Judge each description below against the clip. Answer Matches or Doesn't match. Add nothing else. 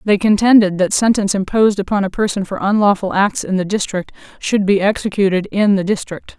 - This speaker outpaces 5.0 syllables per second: Matches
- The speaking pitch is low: Doesn't match